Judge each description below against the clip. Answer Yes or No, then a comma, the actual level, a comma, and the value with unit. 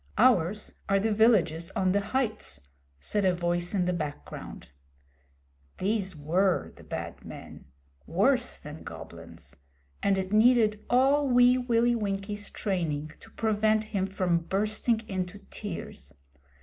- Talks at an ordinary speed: No, slow, 130 wpm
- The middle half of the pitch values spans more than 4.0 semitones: No, average, 3.6 semitones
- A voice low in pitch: No, high, 200 Hz